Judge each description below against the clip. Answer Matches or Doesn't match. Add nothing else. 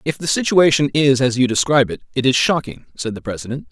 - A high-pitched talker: Doesn't match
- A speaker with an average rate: Doesn't match